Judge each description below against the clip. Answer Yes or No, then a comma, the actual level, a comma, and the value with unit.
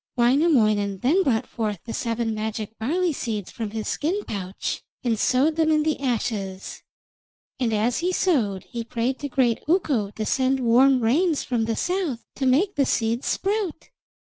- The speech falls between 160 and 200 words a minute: Yes, average, 170 wpm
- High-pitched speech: Yes, high, 245 Hz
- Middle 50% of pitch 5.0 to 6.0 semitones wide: Yes, wide, 5.4 semitones